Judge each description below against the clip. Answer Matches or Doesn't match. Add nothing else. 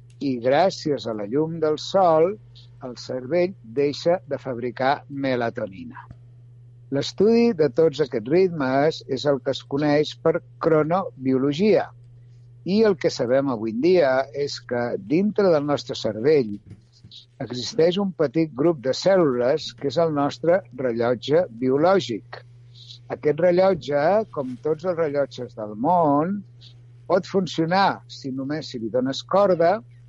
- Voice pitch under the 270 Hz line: Matches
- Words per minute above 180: Doesn't match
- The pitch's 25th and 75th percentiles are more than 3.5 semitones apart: Matches